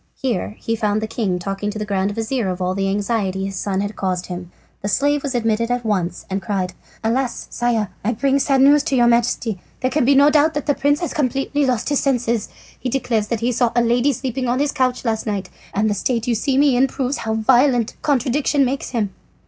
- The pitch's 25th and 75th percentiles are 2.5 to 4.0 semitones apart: No, average, 4.5 semitones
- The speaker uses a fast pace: Yes, fast, 230 wpm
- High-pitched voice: Yes, high, 235 Hz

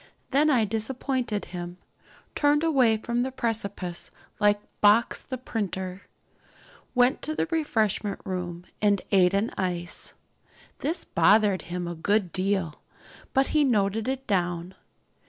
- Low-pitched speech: No, high, 210 Hz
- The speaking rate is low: Yes, slow, 130 wpm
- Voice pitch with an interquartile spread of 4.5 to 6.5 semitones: Yes, average, 5.3 semitones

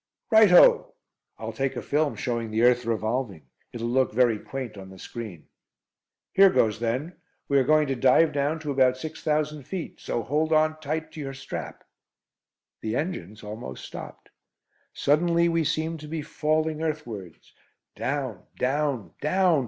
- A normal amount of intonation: Yes, average, 5.0 semitones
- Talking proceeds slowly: No, average, 160 wpm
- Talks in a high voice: No, medium, 140 Hz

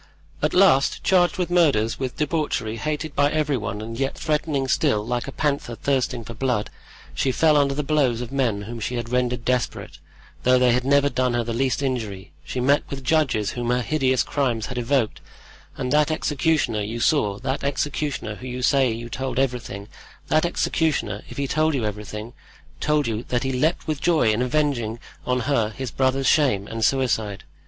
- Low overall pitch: Yes, low, 130 Hz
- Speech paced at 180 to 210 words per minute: Yes, average, 185 wpm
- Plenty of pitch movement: No, average, 3.7 semitones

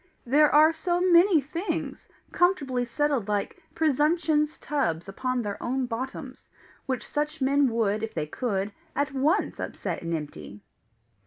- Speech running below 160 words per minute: Yes, average, 140 wpm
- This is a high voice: Yes, very high, 270 Hz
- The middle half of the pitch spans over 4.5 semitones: Yes, average, 5.1 semitones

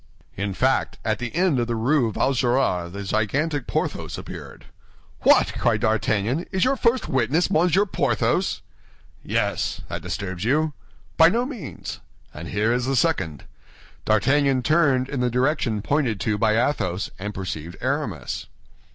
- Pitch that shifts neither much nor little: No, wide, 6.1 semitones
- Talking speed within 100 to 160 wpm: Yes, average, 145 wpm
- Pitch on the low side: Yes, low, 125 Hz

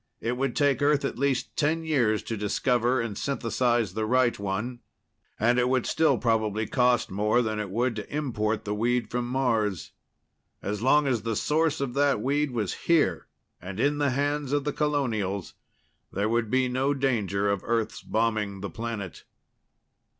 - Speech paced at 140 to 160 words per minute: No, average, 170 wpm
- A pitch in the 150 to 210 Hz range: No, low, 120 Hz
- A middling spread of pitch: Yes, average, 4.2 semitones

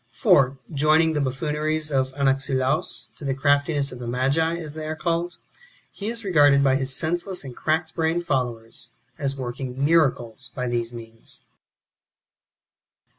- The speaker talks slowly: No, average, 145 wpm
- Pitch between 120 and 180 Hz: Yes, medium, 140 Hz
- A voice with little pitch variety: No, average, 3.4 semitones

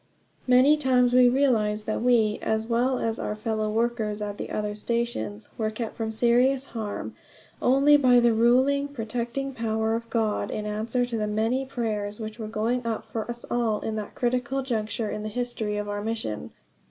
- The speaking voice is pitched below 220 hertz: No, high, 230 Hz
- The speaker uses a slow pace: No, average, 190 wpm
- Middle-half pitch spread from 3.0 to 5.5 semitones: No, narrow, 2.5 semitones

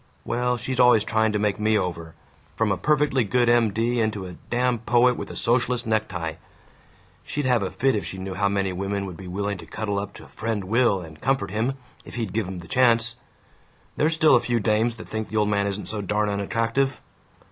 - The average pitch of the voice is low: Yes, low, 110 Hz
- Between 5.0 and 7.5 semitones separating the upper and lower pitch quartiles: No, average, 3.3 semitones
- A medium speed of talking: No, fast, 220 wpm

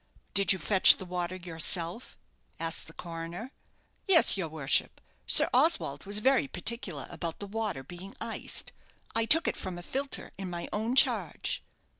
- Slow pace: No, average, 160 wpm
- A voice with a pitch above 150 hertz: Yes, medium, 185 Hz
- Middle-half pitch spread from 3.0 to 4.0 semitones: No, average, 5.0 semitones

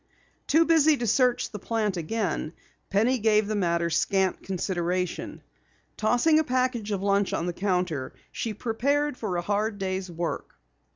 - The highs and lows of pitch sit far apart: No, average, 4.7 semitones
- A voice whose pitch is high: Yes, high, 205 Hz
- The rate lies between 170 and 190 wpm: No, average, 155 wpm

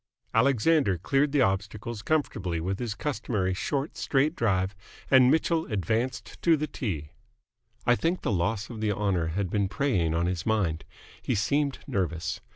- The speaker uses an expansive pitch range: Yes, wide, 6.5 semitones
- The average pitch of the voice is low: Yes, low, 110 Hz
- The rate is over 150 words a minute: Yes, average, 160 wpm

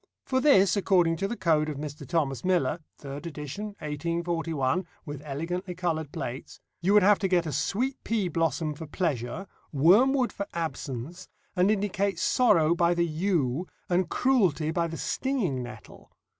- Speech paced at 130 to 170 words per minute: Yes, average, 155 wpm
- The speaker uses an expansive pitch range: No, average, 4.3 semitones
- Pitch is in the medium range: Yes, medium, 170 Hz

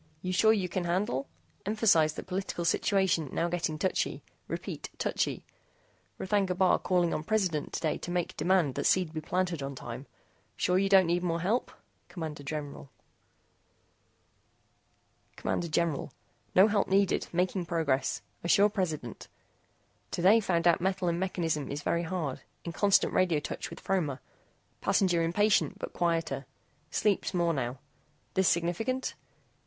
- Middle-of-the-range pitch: Yes, medium, 175 Hz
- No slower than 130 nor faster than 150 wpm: Yes, average, 140 wpm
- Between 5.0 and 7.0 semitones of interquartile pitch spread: No, average, 3.0 semitones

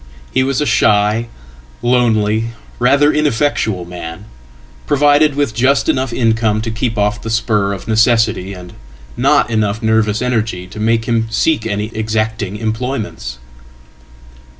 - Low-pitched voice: Yes, low, 110 Hz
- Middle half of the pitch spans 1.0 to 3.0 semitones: Yes, average, 2.7 semitones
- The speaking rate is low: Yes, slow, 125 wpm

